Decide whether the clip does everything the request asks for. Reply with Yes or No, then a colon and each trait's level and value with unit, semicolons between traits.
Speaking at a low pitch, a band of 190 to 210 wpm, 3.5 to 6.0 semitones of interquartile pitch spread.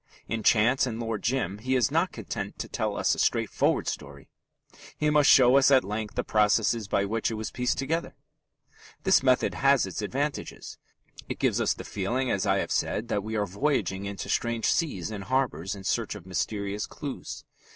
Yes: low, 110 Hz; average, 195 wpm; average, 4.5 semitones